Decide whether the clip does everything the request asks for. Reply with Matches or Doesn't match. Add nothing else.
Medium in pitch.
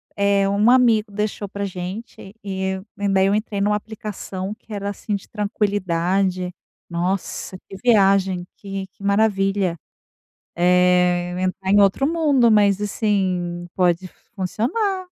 Doesn't match